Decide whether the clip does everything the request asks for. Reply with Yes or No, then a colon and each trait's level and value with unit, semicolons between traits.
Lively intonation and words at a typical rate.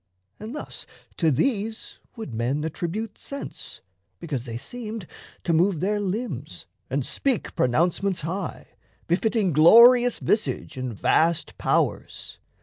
No: wide, 6.0 semitones; slow, 120 wpm